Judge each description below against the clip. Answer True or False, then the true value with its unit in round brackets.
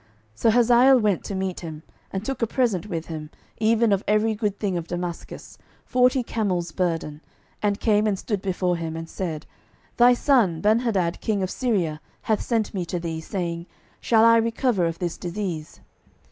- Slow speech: False (180 wpm)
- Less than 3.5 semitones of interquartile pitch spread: False (4.8 semitones)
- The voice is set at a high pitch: True (195 Hz)